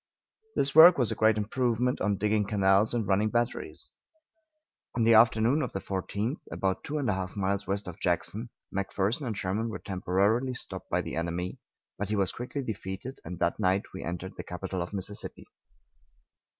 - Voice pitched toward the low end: Yes, low, 105 Hz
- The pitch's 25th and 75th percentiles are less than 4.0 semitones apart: Yes, average, 3.5 semitones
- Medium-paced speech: Yes, average, 180 wpm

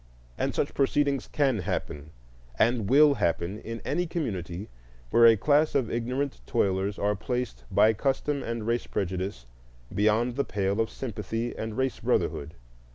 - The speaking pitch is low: Yes, low, 115 Hz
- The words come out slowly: No, average, 150 wpm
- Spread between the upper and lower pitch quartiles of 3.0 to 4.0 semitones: No, average, 5.1 semitones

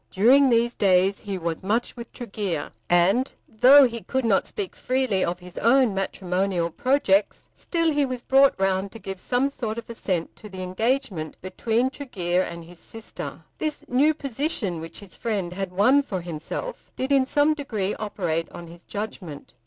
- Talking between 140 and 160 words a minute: No, average, 175 wpm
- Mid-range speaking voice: No, high, 210 Hz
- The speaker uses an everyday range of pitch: No, wide, 6.1 semitones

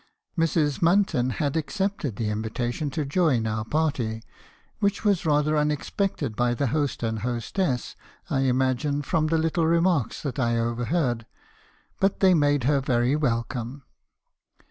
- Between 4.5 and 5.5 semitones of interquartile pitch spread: Yes, average, 5.0 semitones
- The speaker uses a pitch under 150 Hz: Yes, medium, 140 Hz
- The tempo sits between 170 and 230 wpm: No, slow, 135 wpm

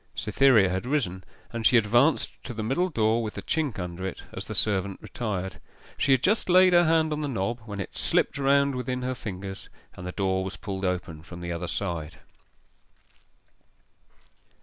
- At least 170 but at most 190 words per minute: Yes, average, 185 wpm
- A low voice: Yes, low, 110 Hz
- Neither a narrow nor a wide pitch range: No, wide, 6.4 semitones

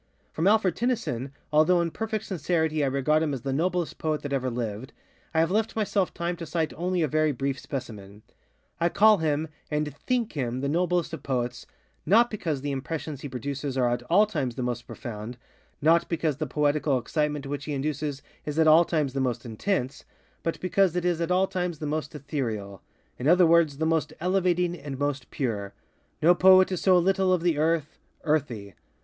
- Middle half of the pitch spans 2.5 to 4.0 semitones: No, average, 4.5 semitones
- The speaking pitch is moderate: Yes, medium, 155 Hz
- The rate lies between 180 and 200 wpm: Yes, average, 190 wpm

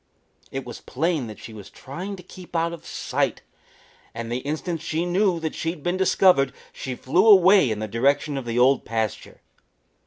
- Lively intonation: Yes, wide, 6.1 semitones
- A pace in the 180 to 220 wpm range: Yes, average, 190 wpm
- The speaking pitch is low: No, medium, 150 Hz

